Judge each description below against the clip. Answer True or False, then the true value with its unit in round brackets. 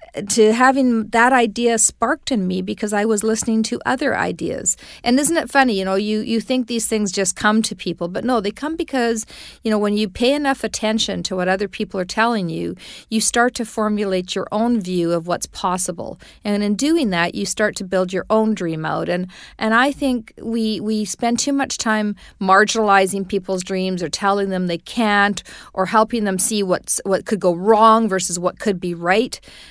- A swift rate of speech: True (210 wpm)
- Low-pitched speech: False (215 Hz)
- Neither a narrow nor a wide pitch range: True (3.3 semitones)